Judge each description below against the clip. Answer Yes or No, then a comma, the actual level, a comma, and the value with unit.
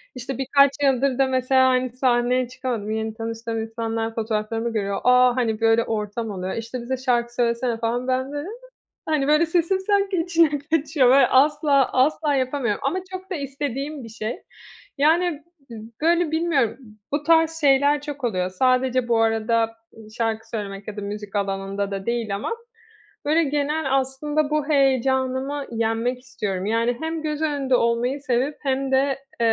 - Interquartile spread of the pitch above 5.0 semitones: No, average, 4.2 semitones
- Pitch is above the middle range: Yes, very high, 255 Hz